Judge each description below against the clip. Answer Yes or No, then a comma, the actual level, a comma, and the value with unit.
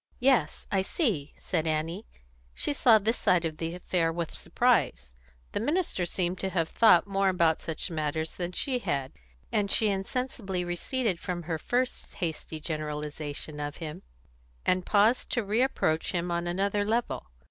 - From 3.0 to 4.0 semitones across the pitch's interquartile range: No, average, 4.7 semitones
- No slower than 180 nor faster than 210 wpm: No, average, 160 wpm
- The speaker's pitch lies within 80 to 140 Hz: No, medium, 180 Hz